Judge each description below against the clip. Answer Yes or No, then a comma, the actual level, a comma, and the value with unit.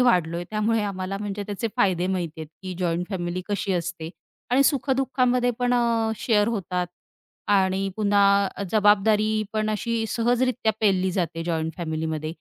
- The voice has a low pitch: No, high, 200 Hz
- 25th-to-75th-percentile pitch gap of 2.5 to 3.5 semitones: No, average, 3.9 semitones